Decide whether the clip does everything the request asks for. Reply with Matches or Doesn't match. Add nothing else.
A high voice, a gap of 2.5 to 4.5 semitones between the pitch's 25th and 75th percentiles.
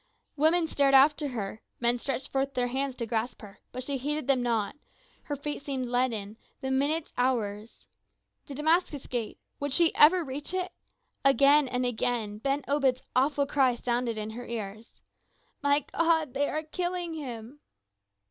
Matches